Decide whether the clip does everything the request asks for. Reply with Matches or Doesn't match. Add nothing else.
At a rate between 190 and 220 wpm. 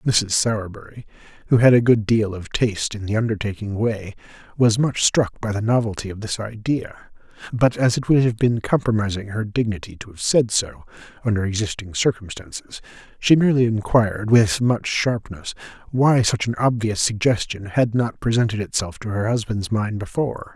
Doesn't match